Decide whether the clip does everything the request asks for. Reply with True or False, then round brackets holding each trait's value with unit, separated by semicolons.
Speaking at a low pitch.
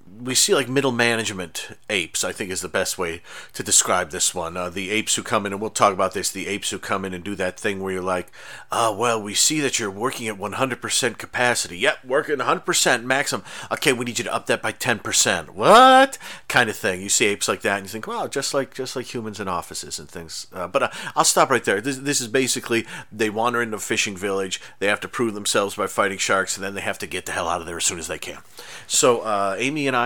True (110 Hz)